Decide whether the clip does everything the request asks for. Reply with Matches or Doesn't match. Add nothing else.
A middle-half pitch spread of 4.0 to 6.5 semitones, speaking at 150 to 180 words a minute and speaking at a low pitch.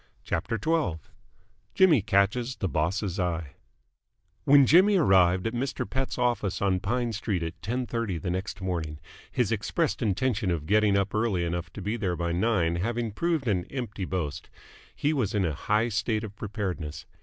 Matches